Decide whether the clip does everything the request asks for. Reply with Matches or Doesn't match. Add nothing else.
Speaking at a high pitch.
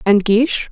Matches